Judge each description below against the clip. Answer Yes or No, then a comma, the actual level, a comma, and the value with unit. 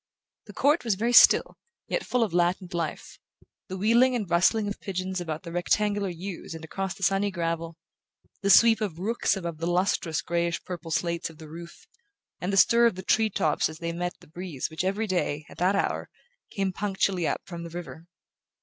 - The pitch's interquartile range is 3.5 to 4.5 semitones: No, average, 3.0 semitones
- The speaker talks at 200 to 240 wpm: Yes, fast, 205 wpm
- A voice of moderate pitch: Yes, medium, 180 Hz